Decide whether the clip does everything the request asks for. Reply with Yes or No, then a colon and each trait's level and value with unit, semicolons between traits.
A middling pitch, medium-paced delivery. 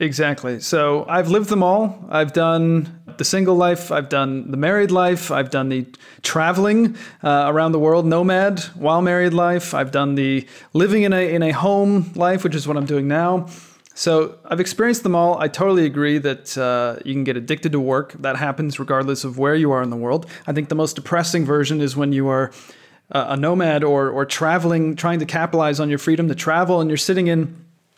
No: medium, 160 Hz; fast, 210 wpm